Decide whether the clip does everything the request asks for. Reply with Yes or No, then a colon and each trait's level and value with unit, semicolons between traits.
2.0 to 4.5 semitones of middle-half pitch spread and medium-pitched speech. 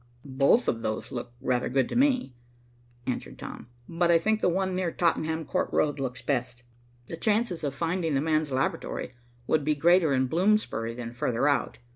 No: average, 5.2 semitones; medium, 150 Hz